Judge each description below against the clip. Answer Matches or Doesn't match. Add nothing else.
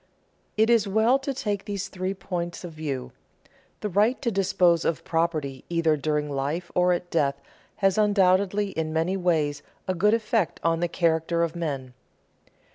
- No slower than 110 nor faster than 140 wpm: Doesn't match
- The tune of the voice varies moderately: Matches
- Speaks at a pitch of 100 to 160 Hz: Doesn't match